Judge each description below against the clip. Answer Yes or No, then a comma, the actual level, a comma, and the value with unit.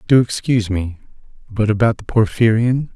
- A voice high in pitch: No, low, 110 Hz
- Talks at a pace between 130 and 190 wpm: Yes, average, 140 wpm